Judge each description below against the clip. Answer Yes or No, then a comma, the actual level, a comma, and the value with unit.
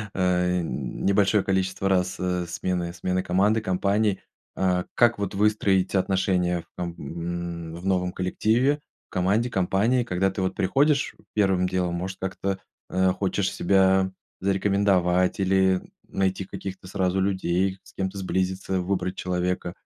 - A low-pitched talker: Yes, very low, 95 Hz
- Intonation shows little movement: Yes, narrow, 1.3 semitones